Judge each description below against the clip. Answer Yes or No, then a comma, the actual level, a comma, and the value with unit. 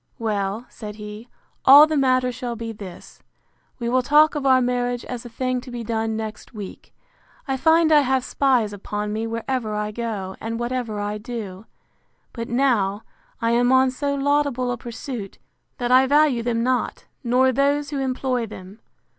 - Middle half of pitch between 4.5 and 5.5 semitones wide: No, average, 3.1 semitones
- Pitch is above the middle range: Yes, high, 245 Hz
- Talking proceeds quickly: No, average, 175 wpm